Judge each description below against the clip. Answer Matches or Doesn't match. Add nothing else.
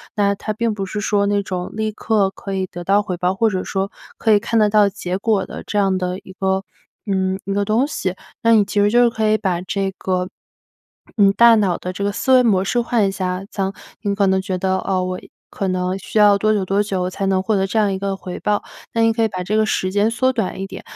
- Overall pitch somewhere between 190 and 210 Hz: Matches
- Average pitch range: Doesn't match